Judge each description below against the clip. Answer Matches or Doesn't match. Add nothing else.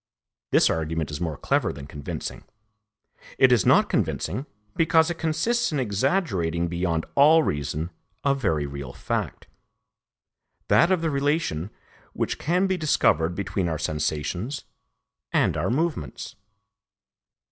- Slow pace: Matches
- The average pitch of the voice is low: Matches